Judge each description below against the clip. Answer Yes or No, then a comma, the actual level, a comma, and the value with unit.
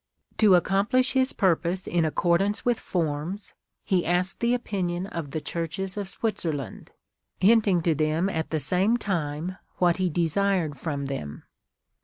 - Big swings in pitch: No, average, 3.7 semitones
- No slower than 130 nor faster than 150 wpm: No, average, 170 wpm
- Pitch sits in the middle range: Yes, medium, 180 Hz